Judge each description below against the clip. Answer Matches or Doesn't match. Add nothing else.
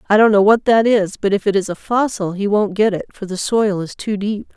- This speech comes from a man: Doesn't match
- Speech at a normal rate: Doesn't match